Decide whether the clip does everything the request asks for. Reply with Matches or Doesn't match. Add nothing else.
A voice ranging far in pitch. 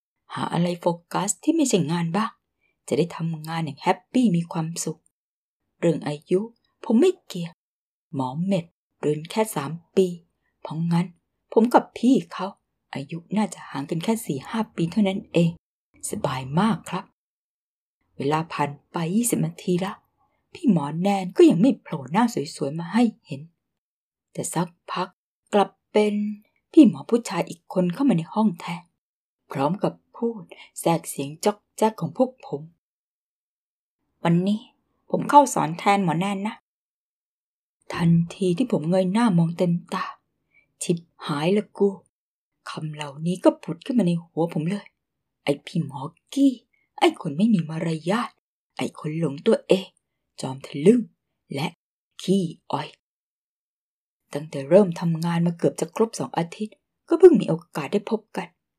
Doesn't match